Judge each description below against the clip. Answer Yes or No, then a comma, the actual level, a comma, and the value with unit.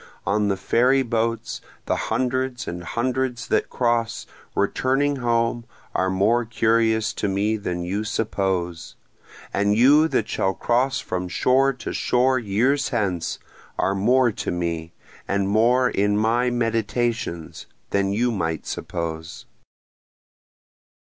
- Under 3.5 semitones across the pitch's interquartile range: No, average, 4.0 semitones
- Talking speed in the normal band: No, slow, 125 wpm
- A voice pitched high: No, low, 115 Hz